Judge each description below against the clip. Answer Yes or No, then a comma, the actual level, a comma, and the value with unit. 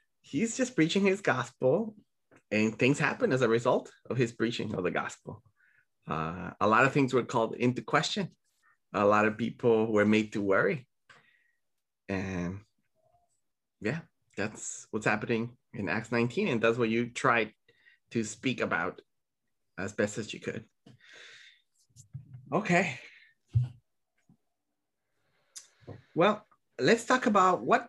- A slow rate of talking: Yes, slow, 130 wpm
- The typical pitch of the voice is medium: No, low, 120 Hz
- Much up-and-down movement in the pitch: Yes, wide, 7.2 semitones